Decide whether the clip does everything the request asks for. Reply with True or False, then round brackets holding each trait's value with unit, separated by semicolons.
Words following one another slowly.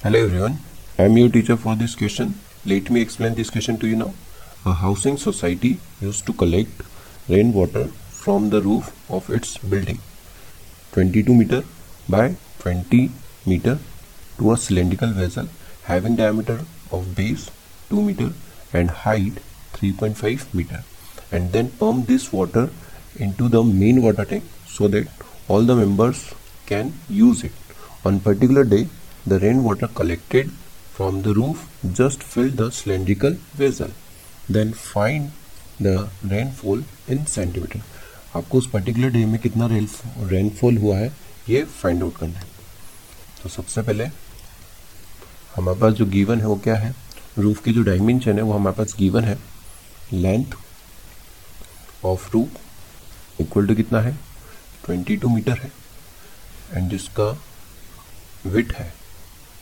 False (140 wpm)